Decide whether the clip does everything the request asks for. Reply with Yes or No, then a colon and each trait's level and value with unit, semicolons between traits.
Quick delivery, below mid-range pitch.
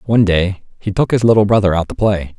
Yes: fast, 250 wpm; low, 100 Hz